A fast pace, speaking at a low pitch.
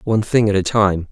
Yes: fast, 270 wpm; low, 100 Hz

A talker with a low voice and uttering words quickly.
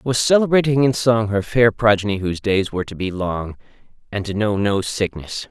No: low, 105 Hz; average, 195 wpm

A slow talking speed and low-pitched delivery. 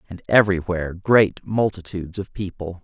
Yes: slow, 125 wpm; very low, 95 Hz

